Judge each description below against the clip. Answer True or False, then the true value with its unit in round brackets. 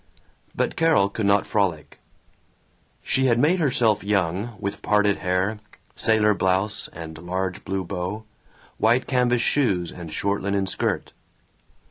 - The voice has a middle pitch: False (100 Hz)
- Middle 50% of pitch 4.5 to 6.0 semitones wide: False (3.3 semitones)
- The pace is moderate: False (130 wpm)